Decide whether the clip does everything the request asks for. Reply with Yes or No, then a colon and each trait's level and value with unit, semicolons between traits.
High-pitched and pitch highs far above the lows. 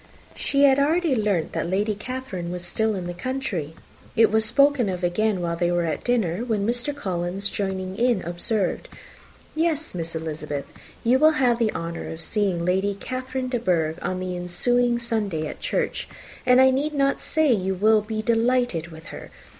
Yes: high, 210 Hz; wide, 6.1 semitones